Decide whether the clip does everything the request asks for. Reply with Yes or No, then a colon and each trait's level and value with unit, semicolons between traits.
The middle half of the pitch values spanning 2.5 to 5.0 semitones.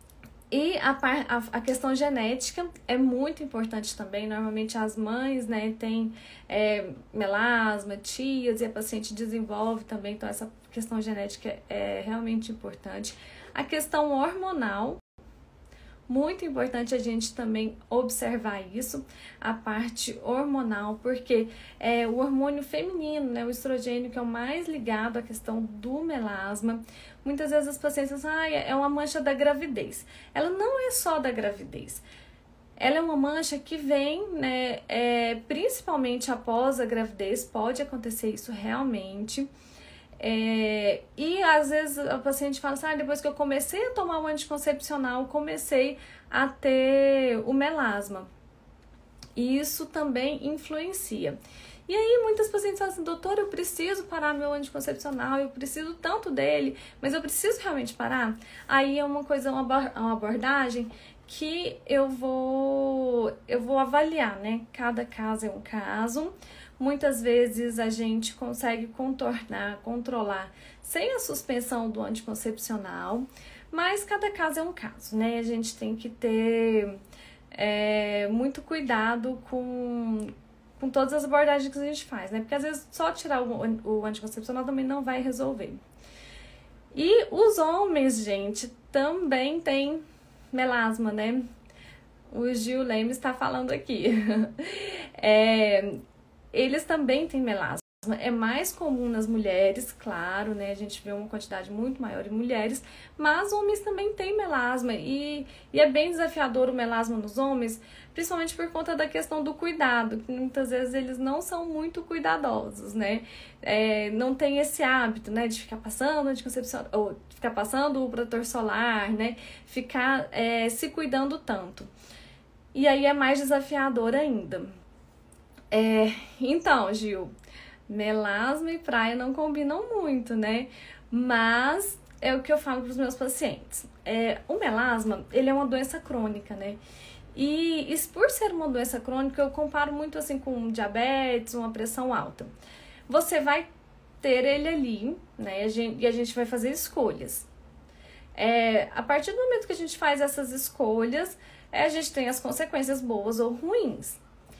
Yes: average, 4.5 semitones